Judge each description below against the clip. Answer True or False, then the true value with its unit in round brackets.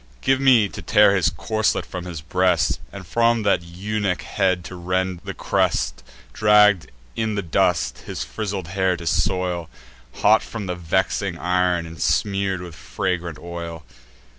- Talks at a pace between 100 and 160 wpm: True (155 wpm)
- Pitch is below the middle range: True (90 Hz)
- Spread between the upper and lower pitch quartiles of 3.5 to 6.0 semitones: False (2.9 semitones)